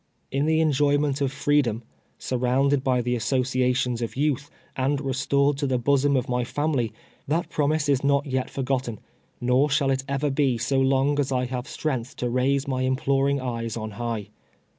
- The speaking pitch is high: No, low, 135 Hz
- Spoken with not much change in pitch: Yes, narrow, 2.1 semitones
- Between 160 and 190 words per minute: Yes, average, 185 wpm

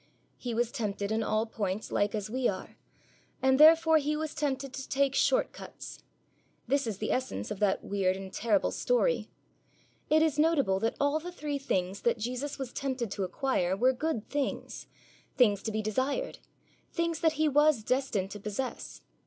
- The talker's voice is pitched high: Yes, very high, 255 Hz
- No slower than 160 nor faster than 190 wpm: Yes, average, 180 wpm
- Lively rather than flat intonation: Yes, wide, 5.8 semitones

